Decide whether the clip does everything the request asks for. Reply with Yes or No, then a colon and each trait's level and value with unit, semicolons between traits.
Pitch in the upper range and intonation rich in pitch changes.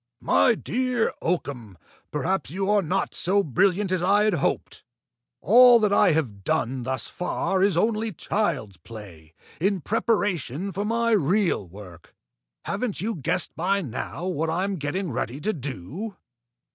No: medium, 180 Hz; wide, 7.2 semitones